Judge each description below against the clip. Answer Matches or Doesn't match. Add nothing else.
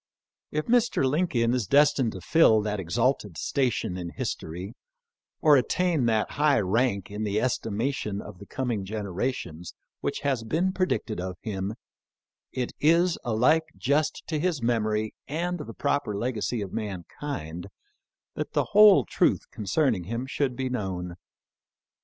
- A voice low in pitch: Matches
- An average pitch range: Doesn't match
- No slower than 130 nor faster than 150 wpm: Matches